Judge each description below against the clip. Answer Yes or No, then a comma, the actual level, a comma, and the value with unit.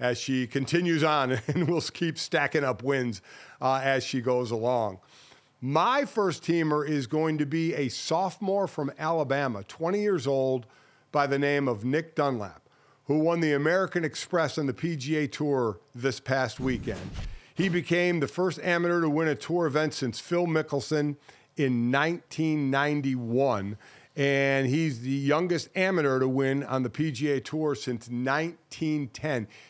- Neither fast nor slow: Yes, average, 150 wpm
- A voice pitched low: No, medium, 145 Hz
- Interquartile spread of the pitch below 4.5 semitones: Yes, average, 3.6 semitones